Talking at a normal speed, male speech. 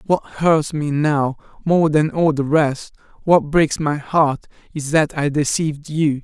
Yes: average, 175 wpm; male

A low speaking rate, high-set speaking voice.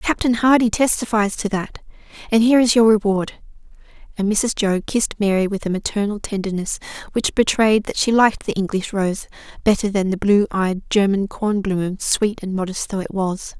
No: average, 175 wpm; high, 205 Hz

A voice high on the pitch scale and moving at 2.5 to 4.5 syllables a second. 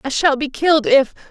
No: very high, 285 Hz; 5.6 syllables/s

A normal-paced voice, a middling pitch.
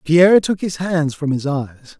No: fast, 210 wpm; medium, 160 Hz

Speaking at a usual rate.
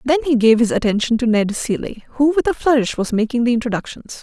No: fast, 225 wpm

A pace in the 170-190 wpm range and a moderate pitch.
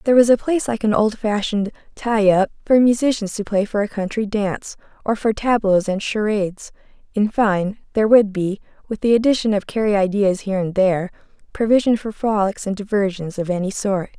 No: average, 185 wpm; high, 210 Hz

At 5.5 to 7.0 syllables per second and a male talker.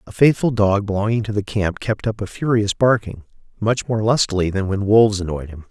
Yes: 5.6 syllables/s; male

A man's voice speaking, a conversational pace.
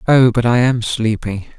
Yes: male; average, 190 wpm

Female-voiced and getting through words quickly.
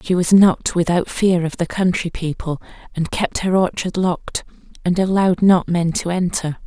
No: female; average, 180 wpm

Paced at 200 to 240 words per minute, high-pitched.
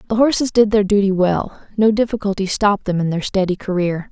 Yes: fast, 205 wpm; high, 200 Hz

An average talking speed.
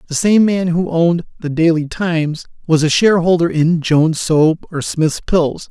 Yes: average, 180 wpm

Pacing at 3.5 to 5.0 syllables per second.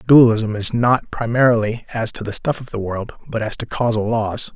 No: 5.4 syllables/s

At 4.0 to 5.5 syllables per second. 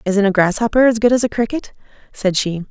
No: 6.1 syllables/s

